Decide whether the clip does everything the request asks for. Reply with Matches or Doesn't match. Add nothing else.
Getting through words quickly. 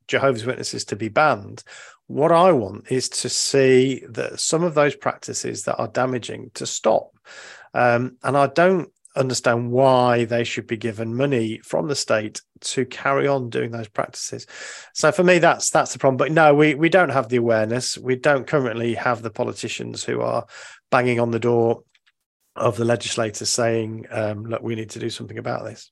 Doesn't match